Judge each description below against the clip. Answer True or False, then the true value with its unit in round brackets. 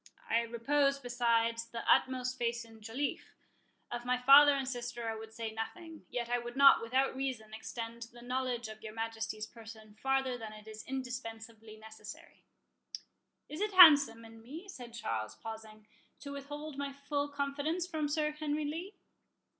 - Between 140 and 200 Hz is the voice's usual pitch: False (245 Hz)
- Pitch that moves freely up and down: False (3.9 semitones)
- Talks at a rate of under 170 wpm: True (160 wpm)